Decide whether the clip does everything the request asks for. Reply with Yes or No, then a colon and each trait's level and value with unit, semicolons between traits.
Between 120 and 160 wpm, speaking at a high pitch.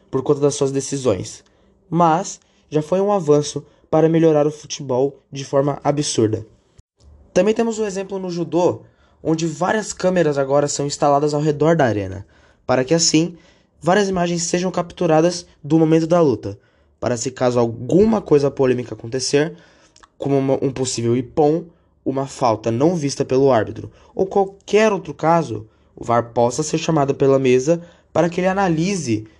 No: average, 155 wpm; medium, 150 Hz